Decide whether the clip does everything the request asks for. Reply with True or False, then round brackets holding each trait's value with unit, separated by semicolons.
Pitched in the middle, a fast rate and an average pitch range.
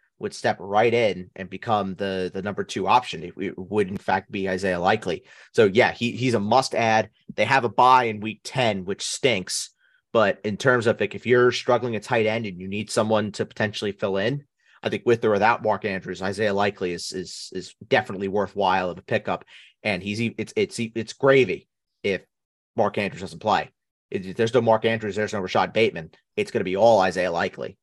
False (105 Hz; 210 wpm; 3.0 semitones)